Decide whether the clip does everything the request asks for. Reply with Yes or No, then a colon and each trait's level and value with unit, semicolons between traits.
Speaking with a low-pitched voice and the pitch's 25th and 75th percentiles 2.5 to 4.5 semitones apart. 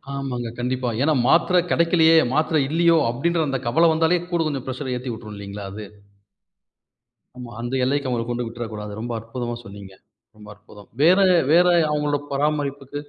No: low, 130 Hz; average, 5.0 semitones